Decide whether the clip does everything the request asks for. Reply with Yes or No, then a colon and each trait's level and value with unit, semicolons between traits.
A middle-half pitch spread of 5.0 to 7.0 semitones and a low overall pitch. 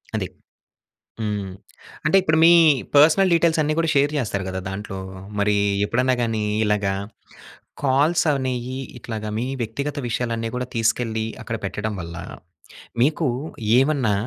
Yes: average, 5.3 semitones; low, 120 Hz